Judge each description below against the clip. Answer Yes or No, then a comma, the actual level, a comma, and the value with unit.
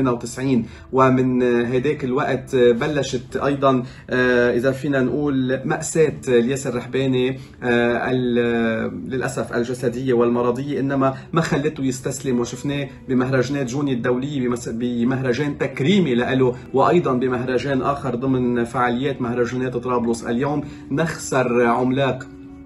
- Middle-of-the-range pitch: No, low, 130 Hz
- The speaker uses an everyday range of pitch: No, narrow, 1.9 semitones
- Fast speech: No, average, 95 wpm